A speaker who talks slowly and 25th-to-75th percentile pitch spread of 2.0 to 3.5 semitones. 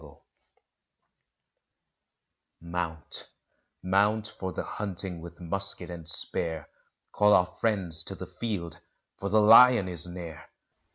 Yes: slow, 115 wpm; average, 3.2 semitones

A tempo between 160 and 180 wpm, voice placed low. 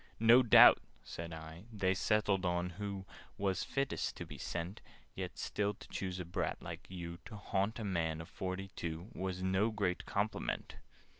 Yes: average, 165 wpm; very low, 95 Hz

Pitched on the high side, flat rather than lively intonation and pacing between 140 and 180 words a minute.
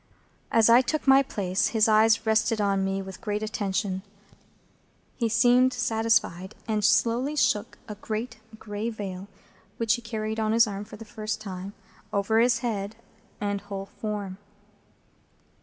Yes: high, 215 Hz; narrow, 2.2 semitones; average, 150 wpm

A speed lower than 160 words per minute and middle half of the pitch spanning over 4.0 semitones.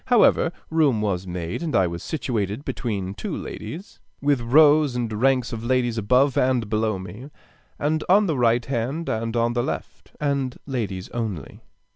No: average, 165 wpm; average, 4.6 semitones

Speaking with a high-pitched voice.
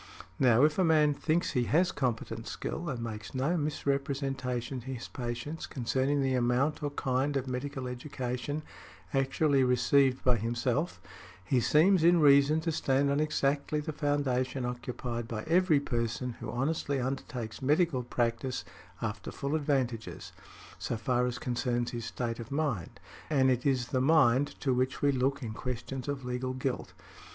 No: low, 130 Hz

